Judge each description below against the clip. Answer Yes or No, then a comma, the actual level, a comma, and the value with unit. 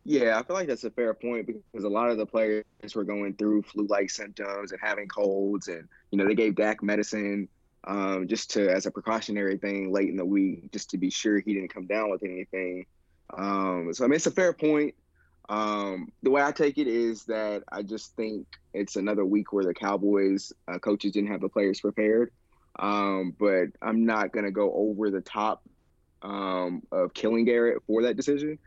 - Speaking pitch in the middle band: No, low, 105 Hz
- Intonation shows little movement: Yes, narrow, 2.0 semitones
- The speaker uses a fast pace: Yes, fast, 210 wpm